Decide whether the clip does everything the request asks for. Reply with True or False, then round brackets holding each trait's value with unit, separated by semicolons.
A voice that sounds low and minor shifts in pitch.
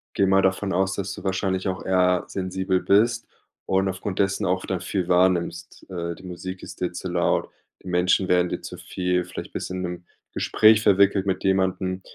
True (95 Hz; 1.2 semitones)